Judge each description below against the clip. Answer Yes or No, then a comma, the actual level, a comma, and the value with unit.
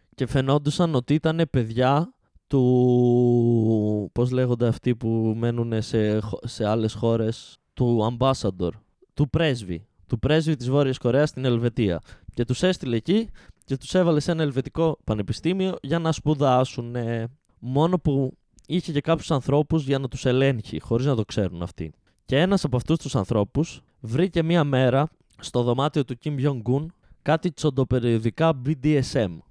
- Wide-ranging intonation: No, average, 4.7 semitones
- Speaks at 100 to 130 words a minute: No, average, 145 wpm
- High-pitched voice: No, low, 130 Hz